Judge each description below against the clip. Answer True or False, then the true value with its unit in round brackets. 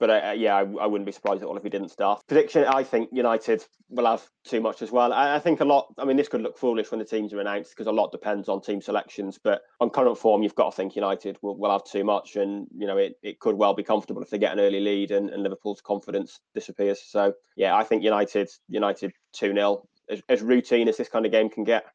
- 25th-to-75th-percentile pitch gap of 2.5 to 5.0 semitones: True (2.9 semitones)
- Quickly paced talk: True (260 wpm)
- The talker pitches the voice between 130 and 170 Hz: False (105 Hz)